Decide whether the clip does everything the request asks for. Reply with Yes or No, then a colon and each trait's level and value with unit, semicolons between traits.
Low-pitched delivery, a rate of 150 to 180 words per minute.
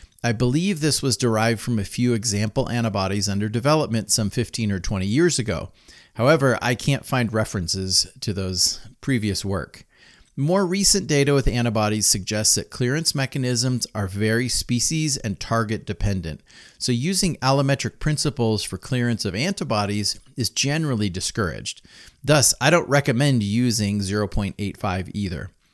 No: low, 115 Hz; average, 140 wpm